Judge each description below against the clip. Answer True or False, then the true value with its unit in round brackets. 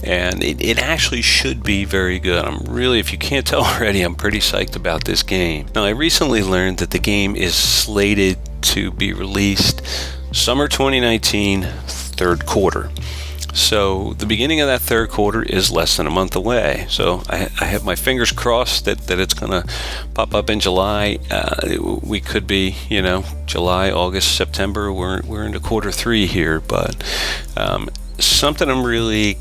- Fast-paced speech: False (180 wpm)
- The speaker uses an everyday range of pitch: False (5.7 semitones)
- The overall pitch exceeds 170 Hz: False (95 Hz)